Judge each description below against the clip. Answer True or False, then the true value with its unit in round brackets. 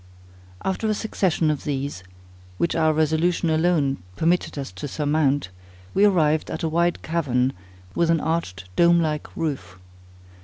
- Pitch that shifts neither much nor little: True (3.1 semitones)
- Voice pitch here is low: False (160 Hz)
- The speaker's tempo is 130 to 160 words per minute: True (145 wpm)